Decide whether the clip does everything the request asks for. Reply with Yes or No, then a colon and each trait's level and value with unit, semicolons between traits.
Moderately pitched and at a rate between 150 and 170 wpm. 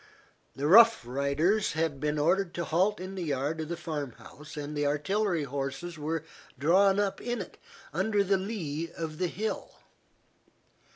Yes: medium, 165 Hz; average, 165 wpm